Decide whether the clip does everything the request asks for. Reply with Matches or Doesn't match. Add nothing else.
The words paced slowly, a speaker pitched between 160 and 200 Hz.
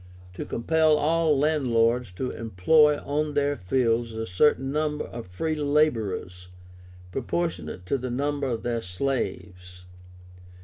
Doesn't match